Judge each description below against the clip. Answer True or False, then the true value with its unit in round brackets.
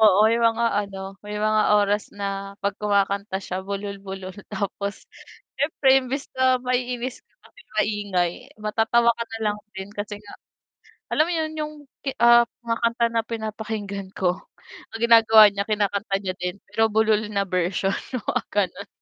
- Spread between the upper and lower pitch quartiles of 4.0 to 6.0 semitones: False (2.6 semitones)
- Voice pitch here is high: True (210 Hz)